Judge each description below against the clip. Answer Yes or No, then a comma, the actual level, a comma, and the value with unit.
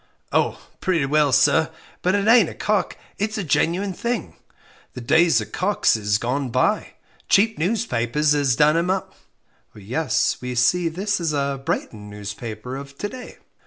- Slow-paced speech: No, average, 165 wpm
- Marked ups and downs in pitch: Yes, wide, 7.2 semitones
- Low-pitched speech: No, medium, 155 Hz